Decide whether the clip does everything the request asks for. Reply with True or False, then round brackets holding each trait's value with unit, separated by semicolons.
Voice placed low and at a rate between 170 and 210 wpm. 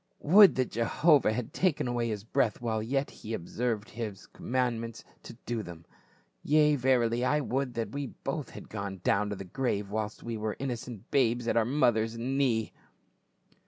True (115 Hz; 175 wpm)